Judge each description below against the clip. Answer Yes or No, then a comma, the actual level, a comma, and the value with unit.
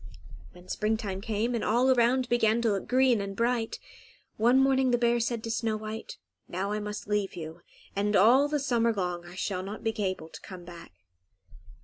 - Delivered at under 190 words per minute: No, average, 195 wpm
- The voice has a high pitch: Yes, high, 220 Hz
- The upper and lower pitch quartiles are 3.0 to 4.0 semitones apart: Yes, average, 3.5 semitones